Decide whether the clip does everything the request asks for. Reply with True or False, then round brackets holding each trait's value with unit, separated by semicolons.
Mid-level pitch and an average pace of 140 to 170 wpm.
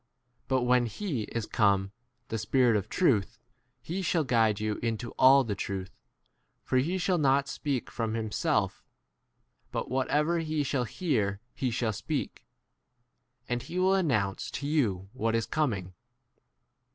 False (125 Hz; 150 wpm)